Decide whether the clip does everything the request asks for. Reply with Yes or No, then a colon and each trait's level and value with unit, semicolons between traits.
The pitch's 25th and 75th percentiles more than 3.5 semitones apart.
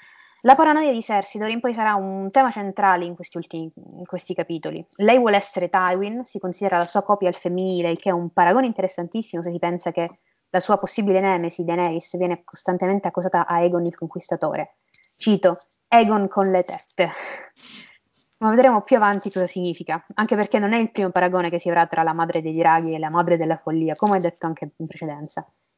No: average, 3.2 semitones